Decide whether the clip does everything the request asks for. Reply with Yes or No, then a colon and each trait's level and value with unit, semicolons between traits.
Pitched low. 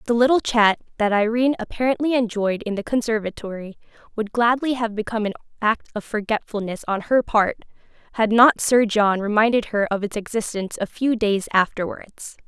No: high, 220 Hz